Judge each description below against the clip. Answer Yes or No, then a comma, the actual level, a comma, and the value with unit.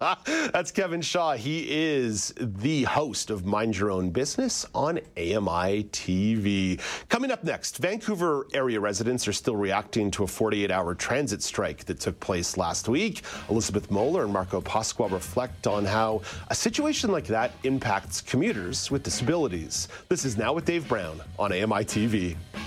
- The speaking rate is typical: Yes, average, 160 wpm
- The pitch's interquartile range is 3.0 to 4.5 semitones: No, wide, 5.4 semitones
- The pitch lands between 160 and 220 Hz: No, low, 110 Hz